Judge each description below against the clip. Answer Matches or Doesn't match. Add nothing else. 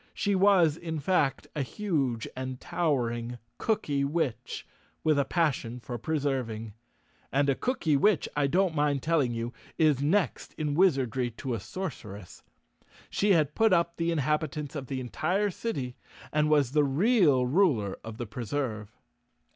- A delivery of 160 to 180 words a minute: Doesn't match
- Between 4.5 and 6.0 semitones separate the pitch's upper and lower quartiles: Matches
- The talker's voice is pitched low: Doesn't match